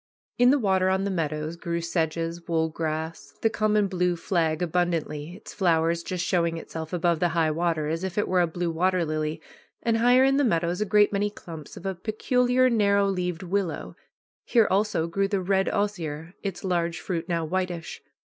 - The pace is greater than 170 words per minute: Yes, average, 190 wpm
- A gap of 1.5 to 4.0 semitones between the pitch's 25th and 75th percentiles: Yes, average, 3.2 semitones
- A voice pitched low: No, medium, 175 Hz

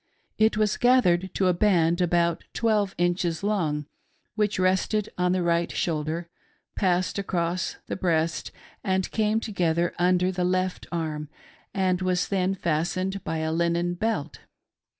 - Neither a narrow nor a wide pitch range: No, narrow, 2.2 semitones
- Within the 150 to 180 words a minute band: No, average, 140 wpm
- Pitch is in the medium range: Yes, medium, 180 Hz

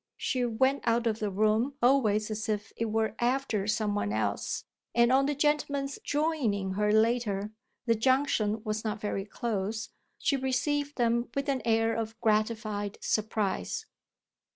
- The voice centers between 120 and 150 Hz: No, high, 225 Hz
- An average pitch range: Yes, average, 3.5 semitones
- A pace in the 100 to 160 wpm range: Yes, average, 155 wpm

